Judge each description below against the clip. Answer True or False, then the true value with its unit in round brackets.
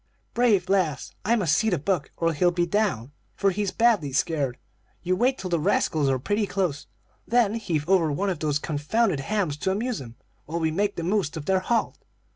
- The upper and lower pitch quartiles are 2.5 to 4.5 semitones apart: False (5.4 semitones)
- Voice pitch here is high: False (180 Hz)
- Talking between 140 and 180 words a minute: False (205 wpm)